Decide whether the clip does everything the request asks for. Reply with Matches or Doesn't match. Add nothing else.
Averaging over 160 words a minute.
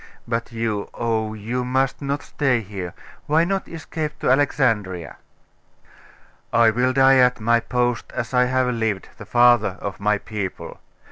Doesn't match